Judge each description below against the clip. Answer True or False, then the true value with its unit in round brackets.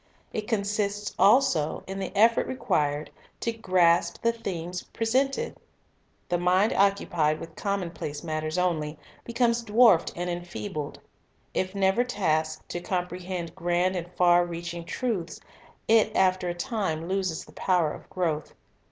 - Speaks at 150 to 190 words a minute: False (135 wpm)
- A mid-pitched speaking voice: True (180 Hz)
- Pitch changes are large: False (3.5 semitones)